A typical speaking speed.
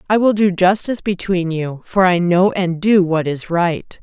No: fast, 210 wpm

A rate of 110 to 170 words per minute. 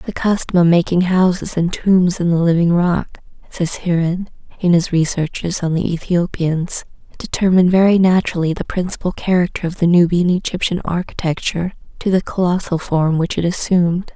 Yes: average, 155 wpm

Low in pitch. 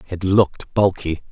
Yes: very low, 90 Hz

